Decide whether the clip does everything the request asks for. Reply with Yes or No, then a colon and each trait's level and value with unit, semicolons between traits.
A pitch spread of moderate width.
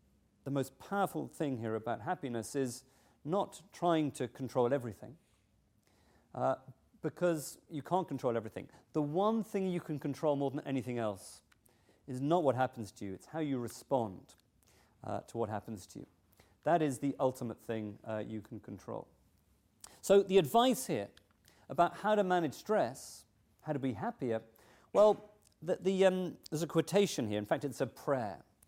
No: wide, 6.8 semitones